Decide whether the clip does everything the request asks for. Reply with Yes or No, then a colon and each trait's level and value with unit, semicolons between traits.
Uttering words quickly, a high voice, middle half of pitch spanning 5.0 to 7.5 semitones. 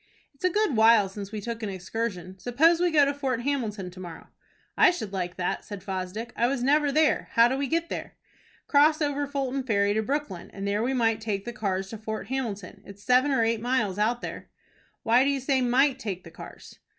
Yes: fast, 225 wpm; high, 230 Hz; wide, 5.5 semitones